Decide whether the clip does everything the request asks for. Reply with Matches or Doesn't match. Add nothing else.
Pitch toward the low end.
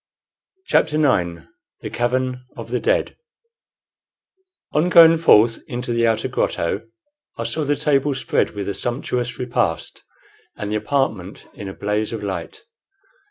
Matches